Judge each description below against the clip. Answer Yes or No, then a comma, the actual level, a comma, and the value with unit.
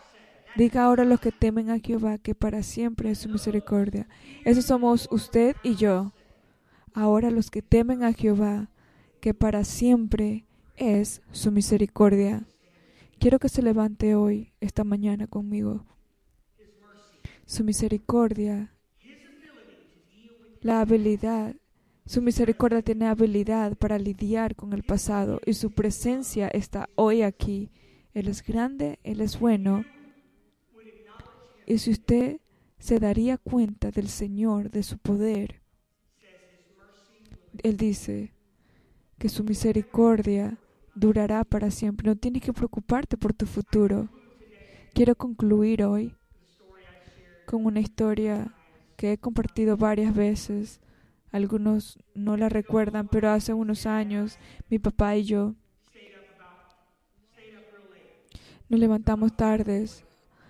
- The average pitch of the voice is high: Yes, high, 215 Hz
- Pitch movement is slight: Yes, narrow, 1.6 semitones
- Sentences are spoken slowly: Yes, slow, 115 wpm